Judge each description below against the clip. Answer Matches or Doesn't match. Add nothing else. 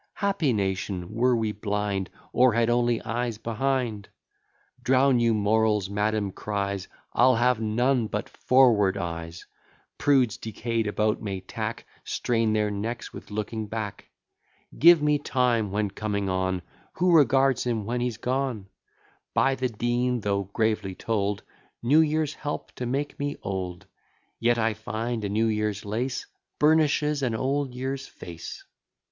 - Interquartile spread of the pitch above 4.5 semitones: Doesn't match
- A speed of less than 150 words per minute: Matches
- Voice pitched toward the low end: Matches